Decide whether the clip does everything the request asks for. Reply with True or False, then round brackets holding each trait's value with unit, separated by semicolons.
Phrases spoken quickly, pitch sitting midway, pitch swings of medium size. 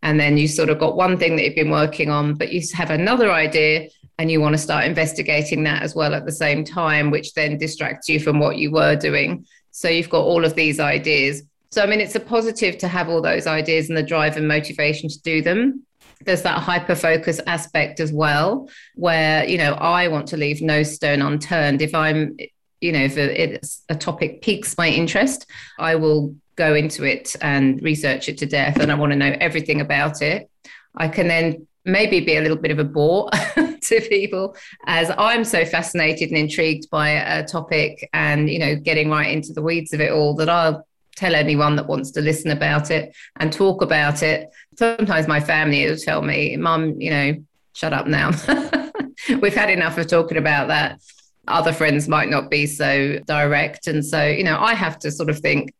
False (210 wpm; 155 Hz; 2.1 semitones)